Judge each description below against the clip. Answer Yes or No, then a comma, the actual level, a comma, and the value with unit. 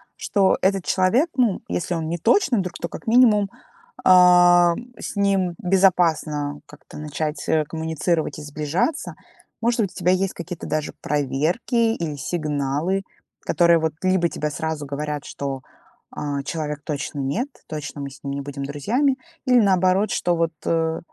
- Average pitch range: Yes, average, 4.3 semitones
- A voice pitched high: No, medium, 170 Hz